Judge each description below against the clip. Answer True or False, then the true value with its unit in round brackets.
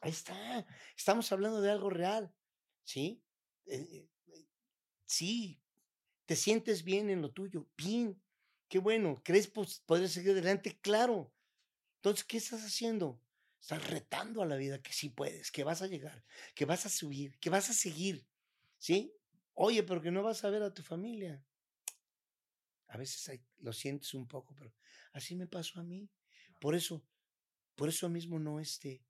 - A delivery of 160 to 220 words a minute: True (165 wpm)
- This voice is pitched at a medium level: True (180 Hz)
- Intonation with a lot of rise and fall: True (5.7 semitones)